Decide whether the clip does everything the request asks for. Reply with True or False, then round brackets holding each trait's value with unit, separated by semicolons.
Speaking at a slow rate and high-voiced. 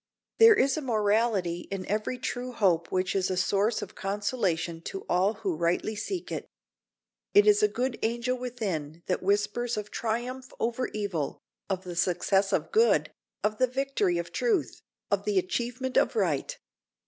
False (165 wpm; 215 Hz)